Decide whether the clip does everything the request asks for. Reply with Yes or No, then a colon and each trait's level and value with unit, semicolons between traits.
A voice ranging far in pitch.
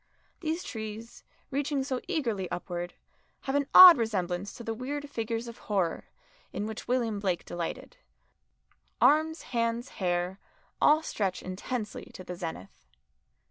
Yes: wide, 6.4 semitones